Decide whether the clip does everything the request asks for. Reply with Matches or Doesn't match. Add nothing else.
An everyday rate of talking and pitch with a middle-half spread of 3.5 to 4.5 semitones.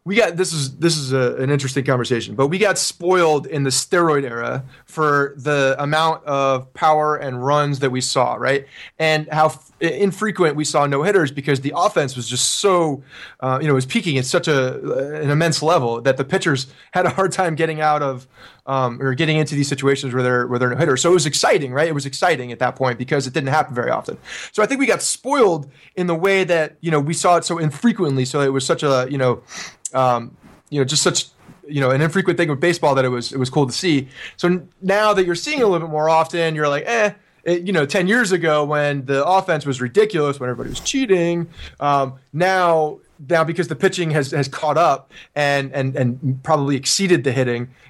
Doesn't match